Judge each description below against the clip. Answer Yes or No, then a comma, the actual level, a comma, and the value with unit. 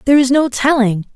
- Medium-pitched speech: No, very high, 260 Hz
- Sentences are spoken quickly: Yes, fast, 210 wpm